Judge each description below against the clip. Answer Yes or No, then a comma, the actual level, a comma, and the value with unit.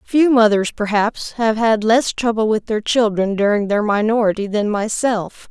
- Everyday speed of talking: Yes, average, 165 wpm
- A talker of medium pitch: No, high, 215 Hz